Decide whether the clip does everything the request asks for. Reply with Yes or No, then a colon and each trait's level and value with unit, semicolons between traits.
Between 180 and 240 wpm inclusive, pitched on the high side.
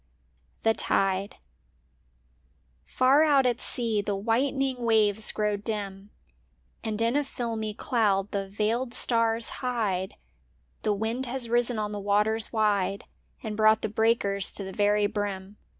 No: slow, 135 wpm; high, 220 Hz